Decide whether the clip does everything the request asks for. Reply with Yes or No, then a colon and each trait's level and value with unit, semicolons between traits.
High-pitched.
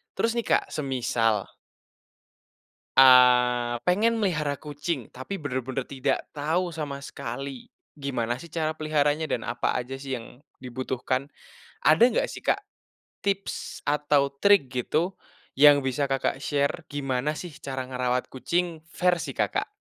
No: medium, 140 Hz